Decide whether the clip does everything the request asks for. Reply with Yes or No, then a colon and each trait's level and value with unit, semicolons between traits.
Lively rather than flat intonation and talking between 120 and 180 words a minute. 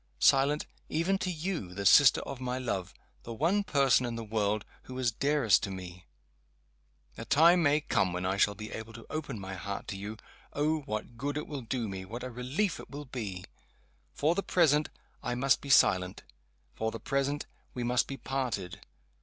No: wide, 5.7 semitones; average, 195 wpm